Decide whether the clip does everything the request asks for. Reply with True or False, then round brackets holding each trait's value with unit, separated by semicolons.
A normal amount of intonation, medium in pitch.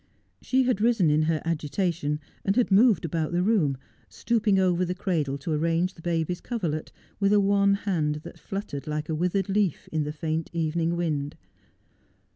True (4.3 semitones; 170 Hz)